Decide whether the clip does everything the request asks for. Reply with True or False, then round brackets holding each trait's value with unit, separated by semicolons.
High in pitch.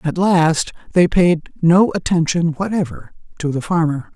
False (170 Hz)